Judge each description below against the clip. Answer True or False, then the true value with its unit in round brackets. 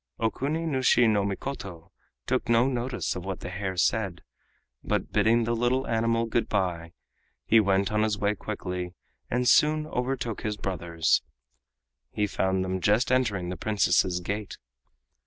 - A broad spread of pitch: False (4.2 semitones)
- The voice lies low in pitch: True (105 Hz)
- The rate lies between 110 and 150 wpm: True (140 wpm)